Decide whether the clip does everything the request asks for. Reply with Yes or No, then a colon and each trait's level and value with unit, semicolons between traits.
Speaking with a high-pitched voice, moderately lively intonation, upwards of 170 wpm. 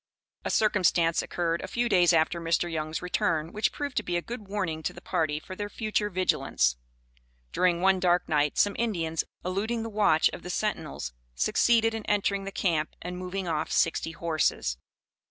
No: medium, 180 Hz; average, 4.1 semitones; average, 180 wpm